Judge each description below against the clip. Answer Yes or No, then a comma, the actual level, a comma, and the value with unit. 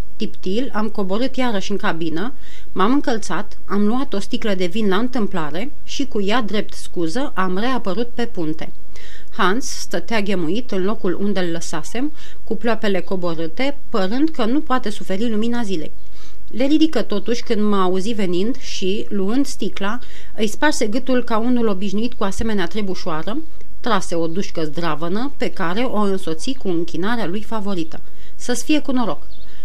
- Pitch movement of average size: Yes, average, 4.7 semitones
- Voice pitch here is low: No, high, 210 Hz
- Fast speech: No, average, 160 wpm